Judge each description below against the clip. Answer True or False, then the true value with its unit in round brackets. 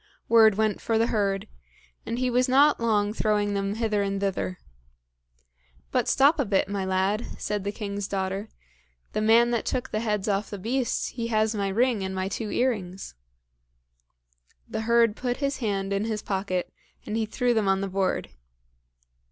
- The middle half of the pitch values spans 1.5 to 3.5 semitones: True (2.8 semitones)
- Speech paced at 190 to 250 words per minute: False (175 wpm)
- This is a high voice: True (210 Hz)